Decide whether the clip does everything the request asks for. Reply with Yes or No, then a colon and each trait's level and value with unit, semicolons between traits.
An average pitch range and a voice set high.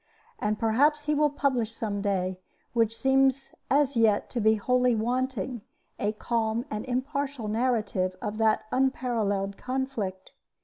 Yes: average, 3.9 semitones; high, 230 Hz